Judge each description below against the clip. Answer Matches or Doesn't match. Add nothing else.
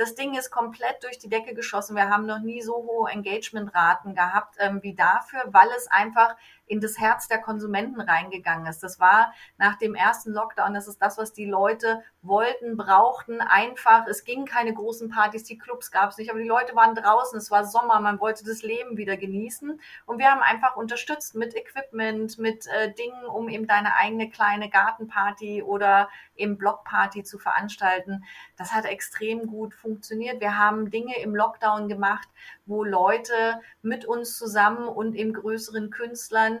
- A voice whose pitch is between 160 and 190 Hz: Doesn't match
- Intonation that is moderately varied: Doesn't match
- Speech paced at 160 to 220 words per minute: Matches